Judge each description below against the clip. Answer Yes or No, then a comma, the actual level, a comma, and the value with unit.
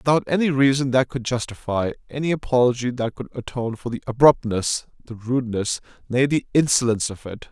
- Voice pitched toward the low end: Yes, low, 125 Hz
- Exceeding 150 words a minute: Yes, average, 170 wpm